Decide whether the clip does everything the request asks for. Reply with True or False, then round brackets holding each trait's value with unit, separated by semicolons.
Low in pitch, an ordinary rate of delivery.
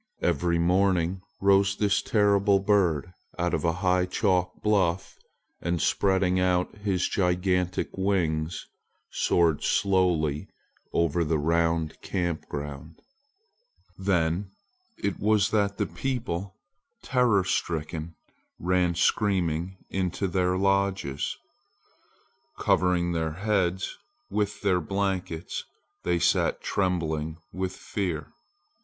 False (90 Hz; 105 wpm)